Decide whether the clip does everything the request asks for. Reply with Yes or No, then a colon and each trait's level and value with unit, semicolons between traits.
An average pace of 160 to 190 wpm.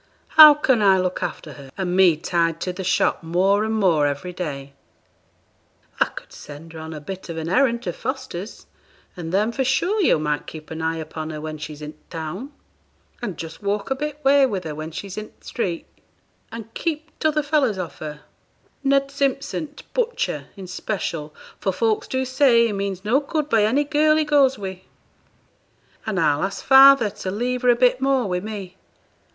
No: average, 200 wpm